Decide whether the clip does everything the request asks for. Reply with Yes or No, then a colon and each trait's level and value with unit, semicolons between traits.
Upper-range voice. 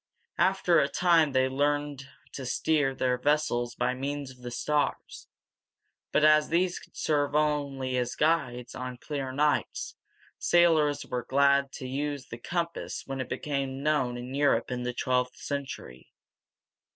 No: medium, 140 Hz